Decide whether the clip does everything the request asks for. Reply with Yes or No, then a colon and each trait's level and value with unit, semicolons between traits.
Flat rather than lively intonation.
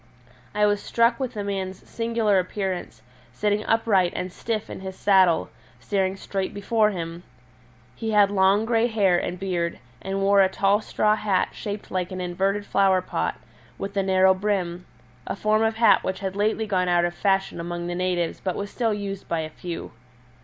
Yes: narrow, 2.3 semitones